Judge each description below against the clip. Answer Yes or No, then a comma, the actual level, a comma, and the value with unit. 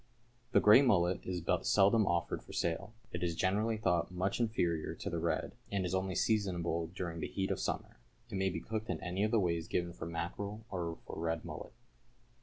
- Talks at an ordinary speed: No, fast, 210 wpm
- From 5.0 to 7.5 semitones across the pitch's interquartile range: No, average, 3.5 semitones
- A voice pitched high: No, very low, 95 Hz